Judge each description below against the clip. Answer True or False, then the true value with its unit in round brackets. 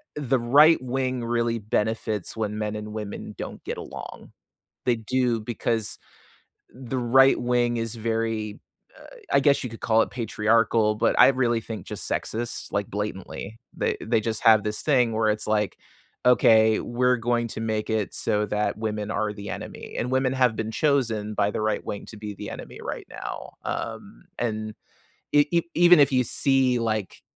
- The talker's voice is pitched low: True (115 Hz)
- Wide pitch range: False (2.6 semitones)